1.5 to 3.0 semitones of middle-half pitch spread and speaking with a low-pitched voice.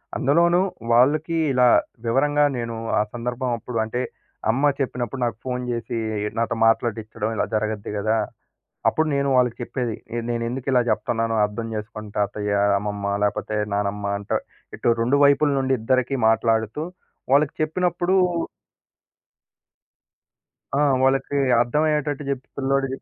No: average, 3.6 semitones; low, 120 Hz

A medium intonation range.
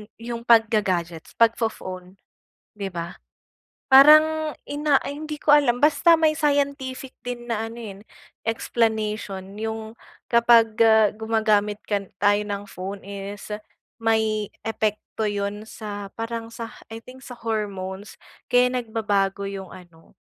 Yes: average, 3.0 semitones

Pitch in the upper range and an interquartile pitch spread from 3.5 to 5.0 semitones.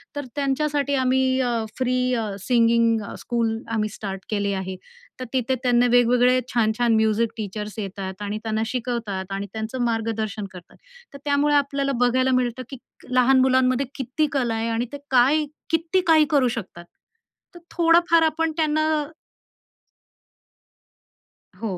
Yes: high, 245 Hz; average, 4.0 semitones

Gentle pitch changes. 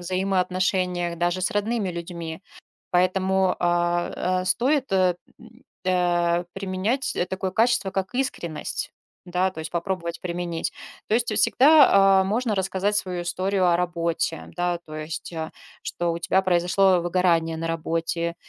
Yes: narrow, 2.0 semitones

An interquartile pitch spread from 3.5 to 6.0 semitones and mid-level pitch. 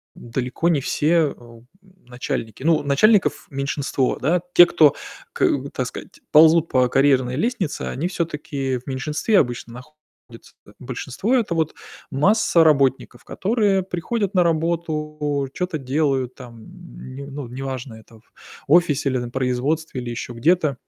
Yes: average, 4.7 semitones; medium, 145 Hz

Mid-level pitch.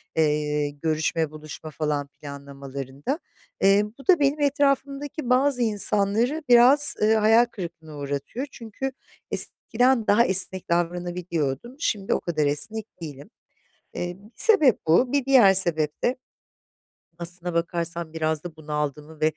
Yes: medium, 175 Hz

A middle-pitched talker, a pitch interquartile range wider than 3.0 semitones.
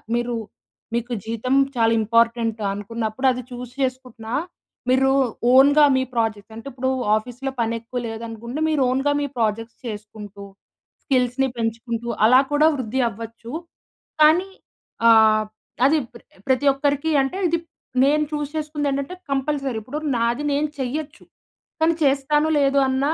No: very high, 250 Hz; average, 3.5 semitones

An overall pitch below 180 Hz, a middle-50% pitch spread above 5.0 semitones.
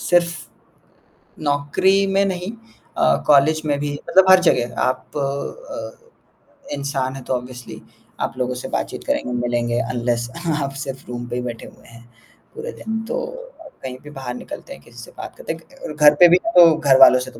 Yes: medium, 140 Hz; wide, 5.4 semitones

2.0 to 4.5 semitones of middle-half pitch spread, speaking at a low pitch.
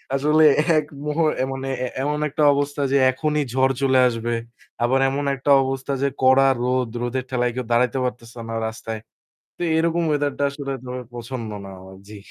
Yes: average, 2.7 semitones; low, 130 Hz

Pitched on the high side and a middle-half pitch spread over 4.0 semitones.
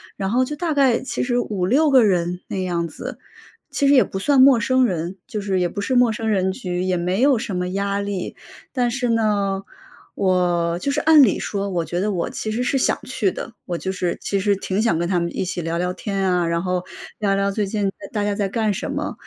Yes: high, 200 Hz; average, 4.7 semitones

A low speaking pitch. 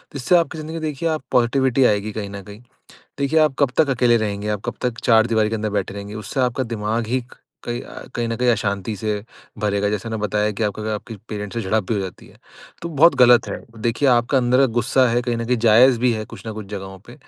Yes: low, 115 Hz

